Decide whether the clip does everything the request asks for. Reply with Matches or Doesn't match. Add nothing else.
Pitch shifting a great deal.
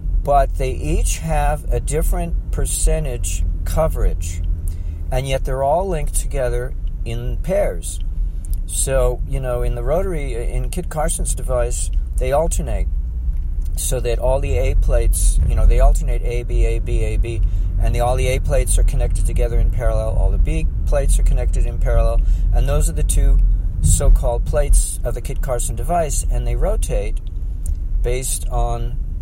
Matches